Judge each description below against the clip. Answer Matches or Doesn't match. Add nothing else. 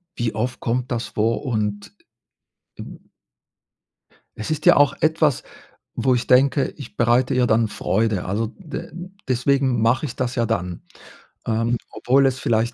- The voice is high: Doesn't match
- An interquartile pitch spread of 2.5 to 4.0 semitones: Matches